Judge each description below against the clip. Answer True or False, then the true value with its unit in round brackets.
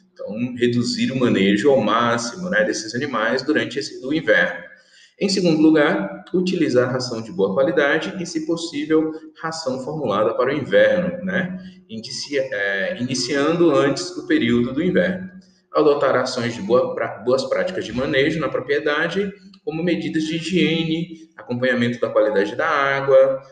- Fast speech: False (145 wpm)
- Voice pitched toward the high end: False (160 Hz)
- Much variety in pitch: True (6.0 semitones)